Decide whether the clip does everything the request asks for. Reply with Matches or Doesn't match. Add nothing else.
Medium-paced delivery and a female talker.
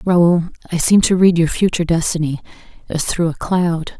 Matches